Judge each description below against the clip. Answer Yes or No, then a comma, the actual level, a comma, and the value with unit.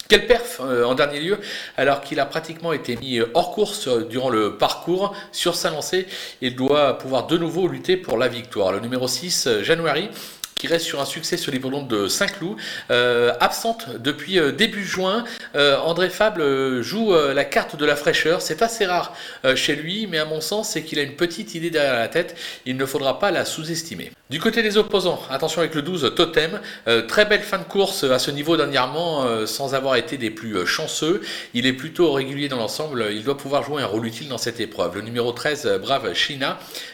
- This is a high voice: No, medium, 155 Hz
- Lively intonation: Yes, wide, 6.1 semitones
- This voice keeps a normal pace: Yes, average, 200 wpm